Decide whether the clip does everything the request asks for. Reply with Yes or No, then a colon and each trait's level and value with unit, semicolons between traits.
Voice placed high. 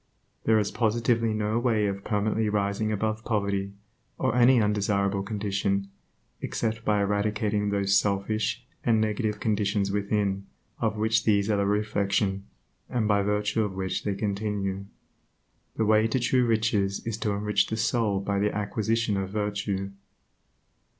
No: low, 105 Hz